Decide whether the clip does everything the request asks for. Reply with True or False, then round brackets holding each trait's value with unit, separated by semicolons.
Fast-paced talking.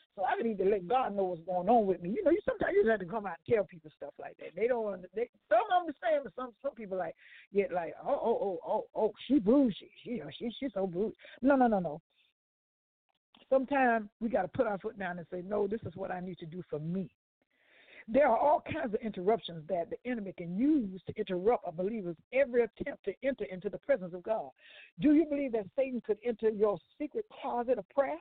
True (240 wpm)